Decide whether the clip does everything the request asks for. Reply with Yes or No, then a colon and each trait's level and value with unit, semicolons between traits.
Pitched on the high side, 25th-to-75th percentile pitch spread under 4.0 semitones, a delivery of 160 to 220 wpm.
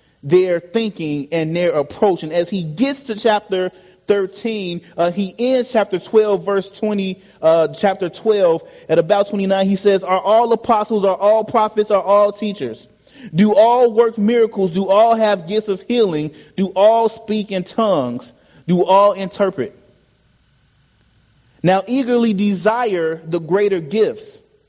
No: high, 200 Hz; average, 3.2 semitones; average, 145 wpm